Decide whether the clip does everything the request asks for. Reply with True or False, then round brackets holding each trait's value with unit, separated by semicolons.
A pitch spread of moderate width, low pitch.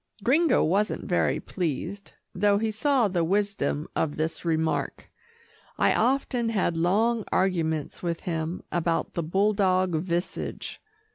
False (4.1 semitones; 185 Hz)